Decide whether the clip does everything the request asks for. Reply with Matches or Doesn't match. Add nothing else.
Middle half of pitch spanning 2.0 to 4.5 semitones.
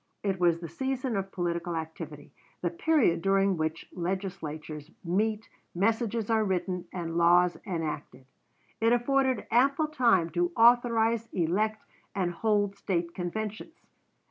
Doesn't match